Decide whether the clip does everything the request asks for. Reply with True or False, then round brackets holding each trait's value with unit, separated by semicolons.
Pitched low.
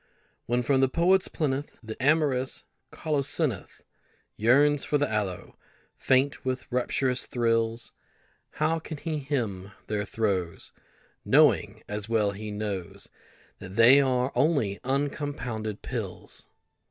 True (125 Hz)